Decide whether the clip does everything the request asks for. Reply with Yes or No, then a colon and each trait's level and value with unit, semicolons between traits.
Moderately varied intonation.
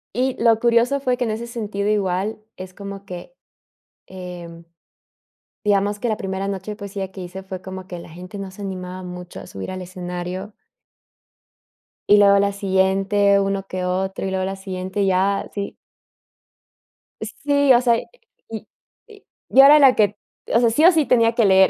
Yes: average, 3.2 semitones